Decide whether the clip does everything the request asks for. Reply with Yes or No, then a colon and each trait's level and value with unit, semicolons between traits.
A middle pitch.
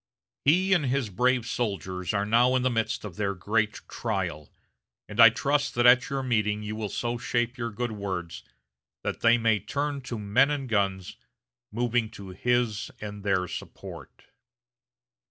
No: low, 115 Hz